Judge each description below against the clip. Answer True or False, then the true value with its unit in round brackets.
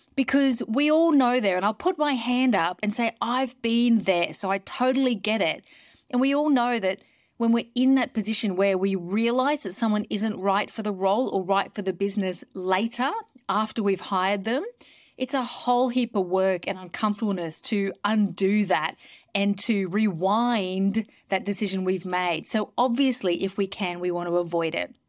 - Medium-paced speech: True (190 wpm)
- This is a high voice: True (210 Hz)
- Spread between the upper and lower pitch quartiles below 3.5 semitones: False (4.3 semitones)